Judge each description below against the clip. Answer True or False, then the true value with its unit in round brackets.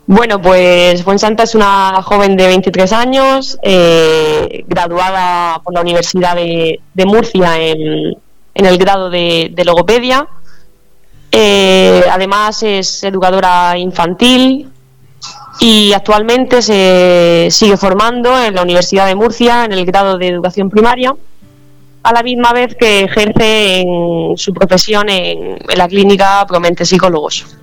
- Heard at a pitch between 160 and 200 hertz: True (190 Hz)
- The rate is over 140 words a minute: False (135 wpm)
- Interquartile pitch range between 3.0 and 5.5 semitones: True (3.4 semitones)